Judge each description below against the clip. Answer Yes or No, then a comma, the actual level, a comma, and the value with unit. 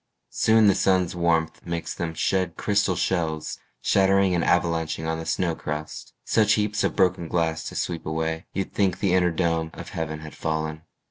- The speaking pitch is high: No, very low, 85 Hz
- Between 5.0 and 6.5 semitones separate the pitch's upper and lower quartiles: No, average, 2.7 semitones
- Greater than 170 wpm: Yes, average, 180 wpm